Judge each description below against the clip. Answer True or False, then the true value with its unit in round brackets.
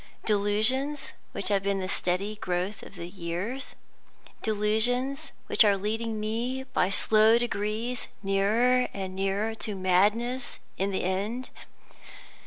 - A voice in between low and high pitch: False (210 Hz)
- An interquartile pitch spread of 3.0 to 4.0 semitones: True (3.3 semitones)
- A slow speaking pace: True (120 wpm)